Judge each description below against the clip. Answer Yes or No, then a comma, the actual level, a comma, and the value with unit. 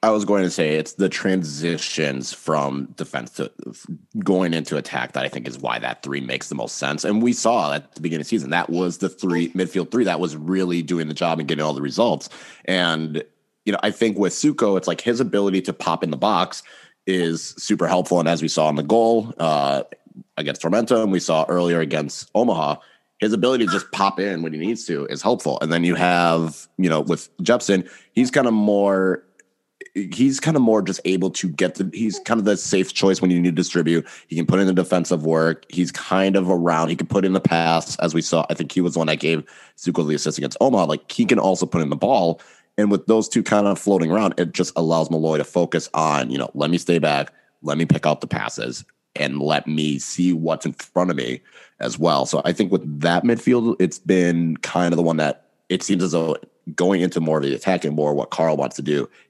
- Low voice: Yes, very low, 85 Hz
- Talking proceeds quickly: Yes, fast, 240 wpm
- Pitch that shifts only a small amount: No, average, 3.1 semitones